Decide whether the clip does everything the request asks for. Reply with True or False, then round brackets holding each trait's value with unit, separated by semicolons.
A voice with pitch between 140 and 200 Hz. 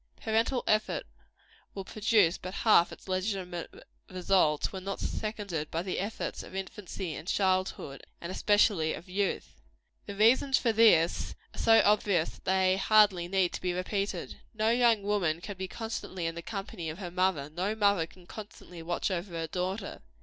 True (190 Hz)